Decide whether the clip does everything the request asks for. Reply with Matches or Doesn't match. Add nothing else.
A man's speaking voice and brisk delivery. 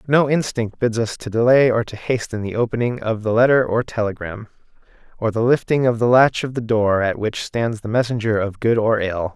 Matches